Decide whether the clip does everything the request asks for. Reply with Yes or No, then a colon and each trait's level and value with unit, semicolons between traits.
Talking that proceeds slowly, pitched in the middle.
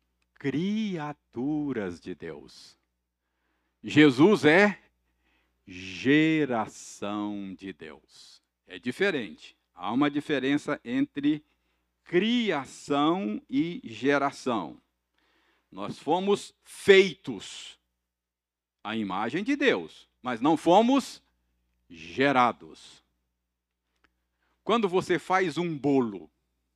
No: slow, 75 wpm; low, 120 Hz